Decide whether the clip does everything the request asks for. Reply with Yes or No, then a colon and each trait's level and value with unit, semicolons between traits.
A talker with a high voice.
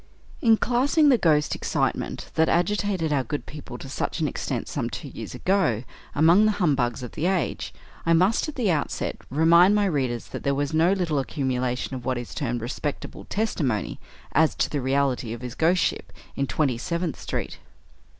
No: medium, 155 Hz